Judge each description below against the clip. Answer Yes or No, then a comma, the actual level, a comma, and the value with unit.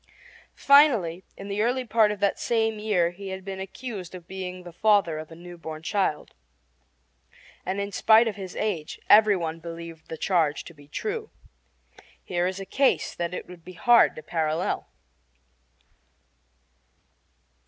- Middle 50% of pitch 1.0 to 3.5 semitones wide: No, average, 4.0 semitones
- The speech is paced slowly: No, average, 160 wpm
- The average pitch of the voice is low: No, high, 190 Hz